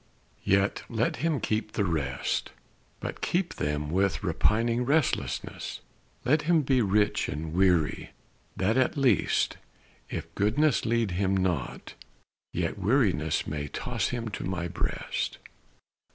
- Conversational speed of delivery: No, slow, 125 wpm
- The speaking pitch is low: Yes, low, 100 Hz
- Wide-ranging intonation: Yes, wide, 5.9 semitones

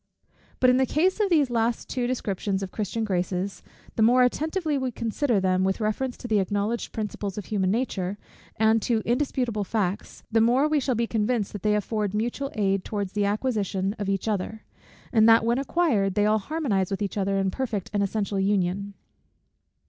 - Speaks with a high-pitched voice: Yes, high, 215 Hz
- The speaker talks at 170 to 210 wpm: Yes, average, 190 wpm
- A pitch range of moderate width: Yes, average, 3.7 semitones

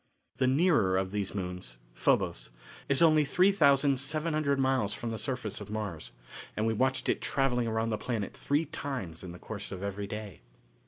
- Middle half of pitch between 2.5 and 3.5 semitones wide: No, wide, 5.6 semitones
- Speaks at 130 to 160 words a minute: No, average, 170 wpm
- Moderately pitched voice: No, low, 115 Hz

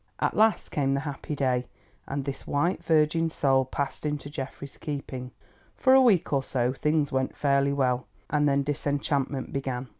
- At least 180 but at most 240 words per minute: No, average, 170 wpm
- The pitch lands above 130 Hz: Yes, medium, 140 Hz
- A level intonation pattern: Yes, narrow, 2.0 semitones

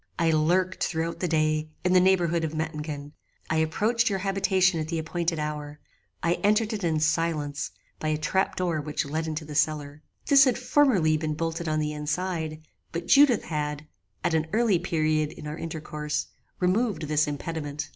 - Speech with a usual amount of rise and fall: Yes, average, 3.0 semitones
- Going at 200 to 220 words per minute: No, average, 175 wpm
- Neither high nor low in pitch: Yes, medium, 160 Hz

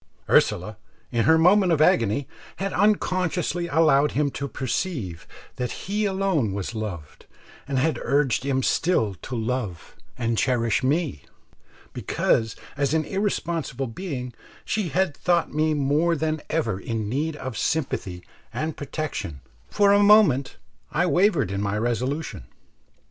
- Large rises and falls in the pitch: Yes, wide, 6.6 semitones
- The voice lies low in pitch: No, medium, 145 Hz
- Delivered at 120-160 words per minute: Yes, average, 140 wpm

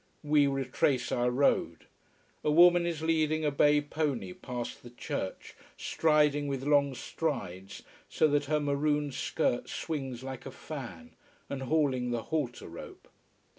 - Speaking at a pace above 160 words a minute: No, average, 140 wpm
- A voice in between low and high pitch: Yes, medium, 145 Hz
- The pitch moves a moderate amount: Yes, average, 3.0 semitones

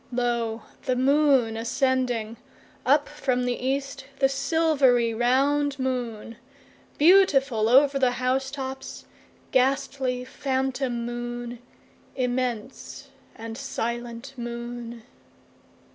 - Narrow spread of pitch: Yes, narrow, 2.3 semitones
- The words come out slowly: Yes, slow, 80 wpm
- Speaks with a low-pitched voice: No, very high, 255 Hz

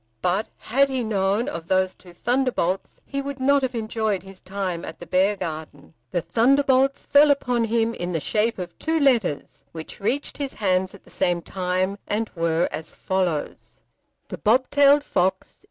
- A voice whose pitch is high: Yes, high, 205 Hz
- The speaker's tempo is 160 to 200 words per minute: Yes, average, 170 wpm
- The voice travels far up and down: Yes, wide, 6.2 semitones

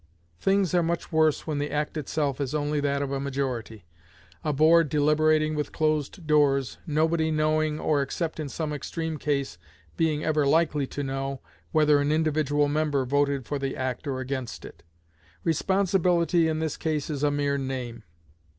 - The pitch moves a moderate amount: No, narrow, 2.1 semitones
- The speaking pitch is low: No, medium, 150 Hz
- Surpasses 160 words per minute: Yes, average, 170 wpm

